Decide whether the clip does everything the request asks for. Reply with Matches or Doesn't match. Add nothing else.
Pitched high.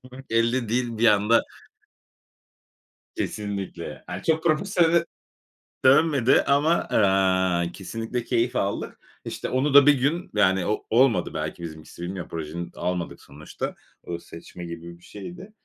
Doesn't match